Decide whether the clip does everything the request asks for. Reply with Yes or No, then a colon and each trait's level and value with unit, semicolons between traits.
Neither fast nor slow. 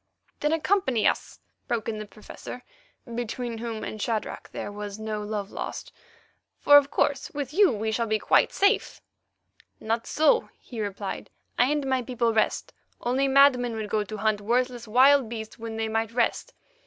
Yes: average, 170 wpm